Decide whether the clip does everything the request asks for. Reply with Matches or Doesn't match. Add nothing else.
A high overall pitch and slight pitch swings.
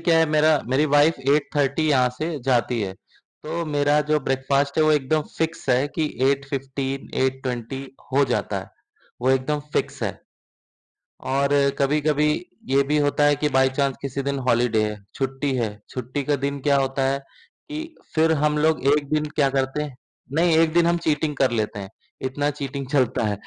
Doesn't match